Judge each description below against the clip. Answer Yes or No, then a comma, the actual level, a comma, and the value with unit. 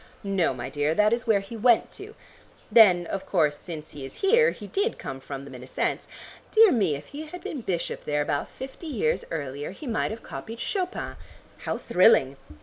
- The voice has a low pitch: No, high, 195 Hz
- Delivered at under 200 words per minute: No, fast, 205 wpm